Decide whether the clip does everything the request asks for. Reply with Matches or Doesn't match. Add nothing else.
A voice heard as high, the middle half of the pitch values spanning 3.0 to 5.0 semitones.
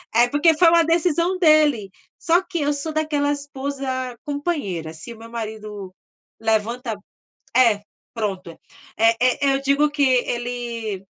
Doesn't match